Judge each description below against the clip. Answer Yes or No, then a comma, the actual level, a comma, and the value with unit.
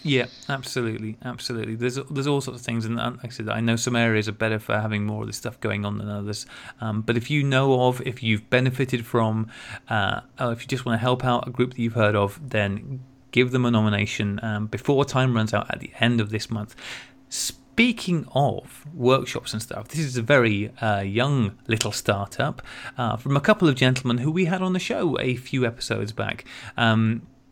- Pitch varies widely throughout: No, average, 3.2 semitones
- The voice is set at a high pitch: No, low, 120 Hz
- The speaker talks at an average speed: No, fast, 220 wpm